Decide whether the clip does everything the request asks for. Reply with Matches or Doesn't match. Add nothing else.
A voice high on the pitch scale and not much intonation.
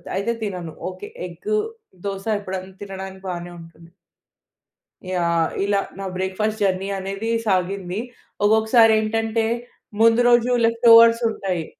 Doesn't match